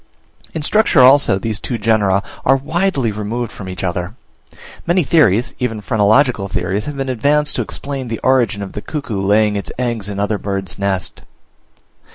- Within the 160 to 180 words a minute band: Yes, average, 175 wpm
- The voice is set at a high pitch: No, low, 110 Hz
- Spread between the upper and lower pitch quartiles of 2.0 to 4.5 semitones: No, average, 5.1 semitones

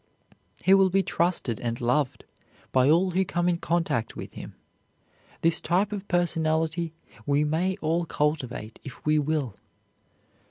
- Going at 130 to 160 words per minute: Yes, average, 145 wpm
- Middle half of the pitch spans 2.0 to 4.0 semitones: Yes, average, 3.4 semitones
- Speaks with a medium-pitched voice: Yes, medium, 160 Hz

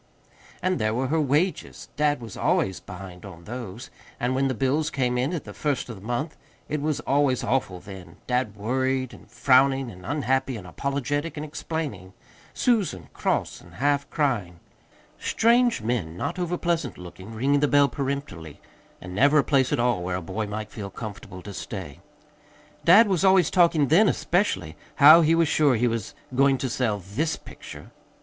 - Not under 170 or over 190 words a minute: Yes, average, 175 wpm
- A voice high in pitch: No, low, 130 Hz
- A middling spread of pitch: No, wide, 6.1 semitones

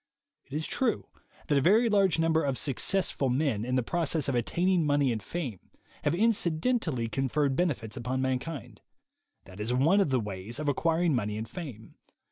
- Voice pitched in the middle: Yes, medium, 145 Hz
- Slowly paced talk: No, average, 180 wpm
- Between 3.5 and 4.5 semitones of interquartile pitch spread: No, wide, 5.5 semitones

